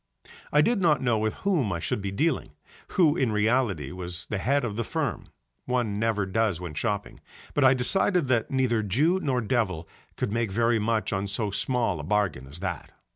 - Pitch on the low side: Yes, low, 110 Hz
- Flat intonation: No, average, 4.8 semitones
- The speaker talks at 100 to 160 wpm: No, average, 195 wpm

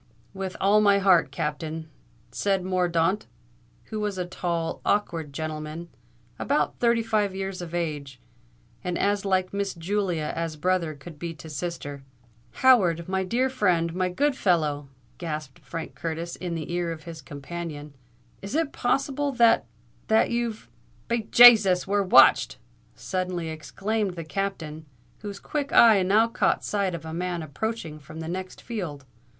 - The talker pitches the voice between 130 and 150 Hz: No, medium, 180 Hz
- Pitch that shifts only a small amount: No, average, 4.1 semitones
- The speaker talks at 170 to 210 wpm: No, average, 145 wpm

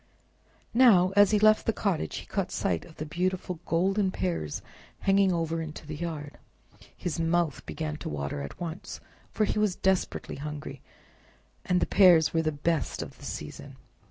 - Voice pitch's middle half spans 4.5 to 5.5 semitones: No, average, 3.7 semitones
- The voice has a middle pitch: Yes, medium, 170 Hz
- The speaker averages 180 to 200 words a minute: No, average, 170 wpm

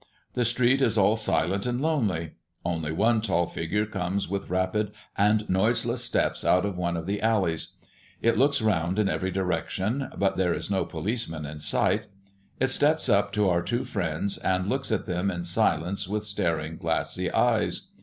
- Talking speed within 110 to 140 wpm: No, average, 175 wpm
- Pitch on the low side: Yes, low, 100 Hz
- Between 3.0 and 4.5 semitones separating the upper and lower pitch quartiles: Yes, average, 4.1 semitones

